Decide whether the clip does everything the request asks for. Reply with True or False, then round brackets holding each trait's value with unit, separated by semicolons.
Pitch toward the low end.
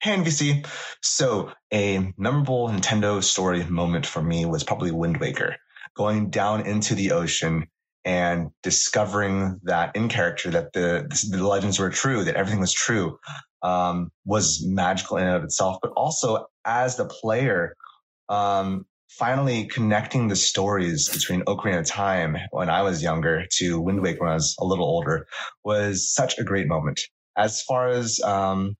True (100 Hz)